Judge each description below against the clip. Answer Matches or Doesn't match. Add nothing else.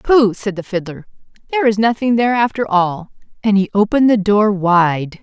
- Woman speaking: Matches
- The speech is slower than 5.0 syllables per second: Doesn't match